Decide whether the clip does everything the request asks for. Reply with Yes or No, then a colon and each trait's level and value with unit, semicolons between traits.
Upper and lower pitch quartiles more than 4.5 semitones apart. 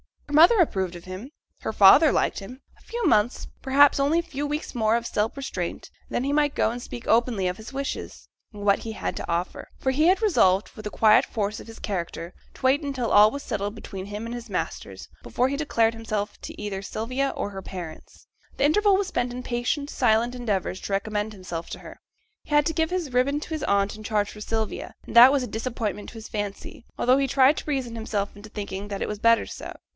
Yes: average, 5.1 semitones